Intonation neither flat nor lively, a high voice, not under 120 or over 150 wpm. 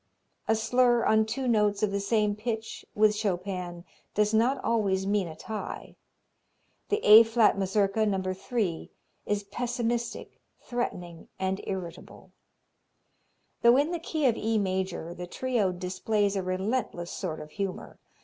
Yes: average, 3.3 semitones; high, 210 Hz; average, 140 wpm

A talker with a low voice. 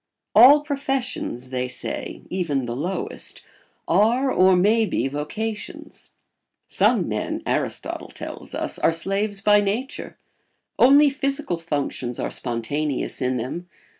No: medium, 185 Hz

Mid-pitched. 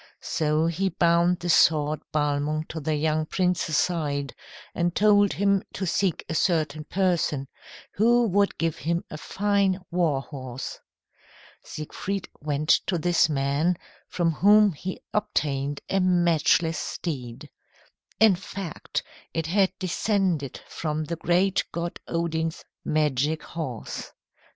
Yes: medium, 165 Hz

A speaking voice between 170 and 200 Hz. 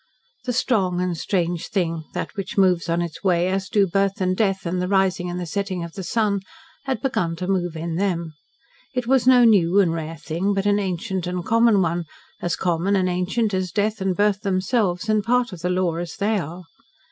Yes: medium, 185 Hz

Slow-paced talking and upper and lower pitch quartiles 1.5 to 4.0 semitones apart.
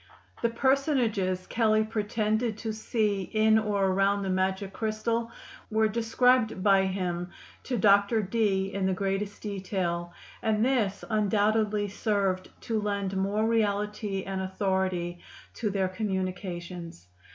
Yes: slow, 125 wpm; narrow, 2.5 semitones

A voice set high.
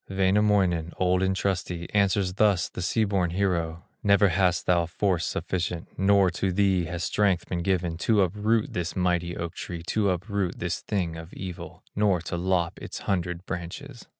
No: very low, 90 Hz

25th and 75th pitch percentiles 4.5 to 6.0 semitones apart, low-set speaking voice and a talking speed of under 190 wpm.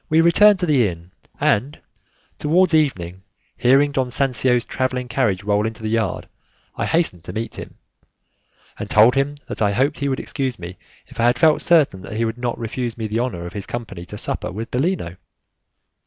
No: average, 5.0 semitones; low, 120 Hz; average, 195 wpm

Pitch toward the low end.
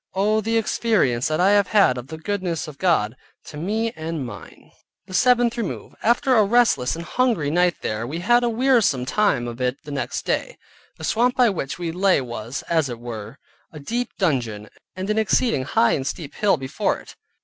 No: medium, 170 Hz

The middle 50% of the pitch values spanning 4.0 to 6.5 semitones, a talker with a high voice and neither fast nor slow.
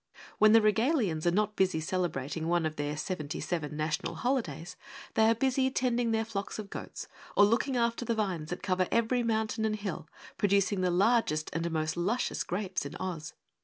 Yes: wide, 5.4 semitones; high, 195 Hz; average, 185 wpm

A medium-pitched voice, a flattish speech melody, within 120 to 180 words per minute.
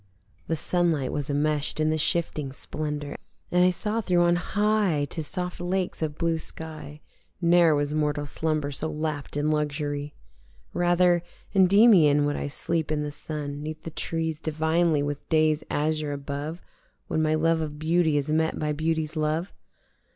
Yes: medium, 155 Hz; narrow, 2.3 semitones; average, 160 wpm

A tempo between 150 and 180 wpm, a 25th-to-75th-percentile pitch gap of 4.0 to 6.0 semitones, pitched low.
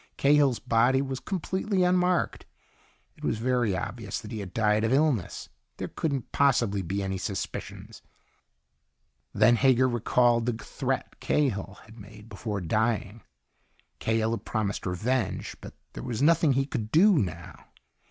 No: average, 140 wpm; average, 4.5 semitones; low, 115 Hz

